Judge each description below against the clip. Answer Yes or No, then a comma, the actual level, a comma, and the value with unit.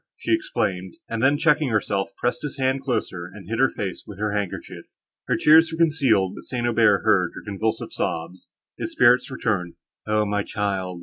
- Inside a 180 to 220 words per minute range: Yes, average, 185 wpm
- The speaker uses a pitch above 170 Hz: No, low, 110 Hz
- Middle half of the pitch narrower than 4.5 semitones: No, average, 5.3 semitones